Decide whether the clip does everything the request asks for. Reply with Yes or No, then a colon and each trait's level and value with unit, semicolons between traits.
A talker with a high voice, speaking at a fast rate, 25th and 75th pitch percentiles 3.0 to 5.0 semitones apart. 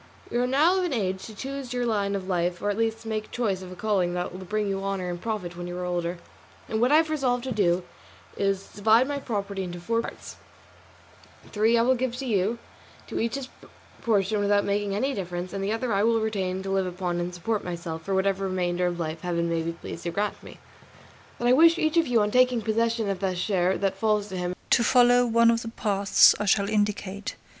Yes: high, 205 Hz; fast, 235 wpm; average, 4.1 semitones